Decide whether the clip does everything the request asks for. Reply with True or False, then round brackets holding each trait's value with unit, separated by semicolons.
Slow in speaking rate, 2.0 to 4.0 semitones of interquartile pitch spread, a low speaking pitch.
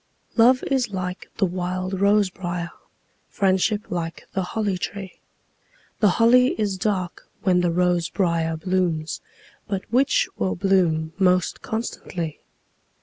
False (125 wpm; 2.7 semitones; 185 Hz)